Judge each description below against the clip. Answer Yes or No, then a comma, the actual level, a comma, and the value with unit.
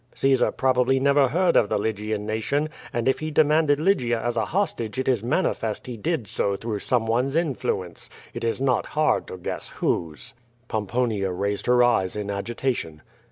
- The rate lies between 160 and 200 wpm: Yes, average, 170 wpm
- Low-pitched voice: Yes, low, 120 Hz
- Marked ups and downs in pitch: No, average, 4.6 semitones